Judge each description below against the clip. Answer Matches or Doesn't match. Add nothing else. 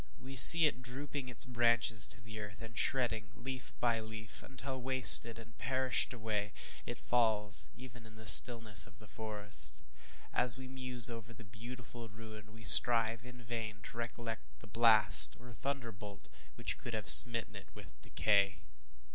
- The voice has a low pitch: Matches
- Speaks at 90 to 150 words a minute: Doesn't match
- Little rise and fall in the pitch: Matches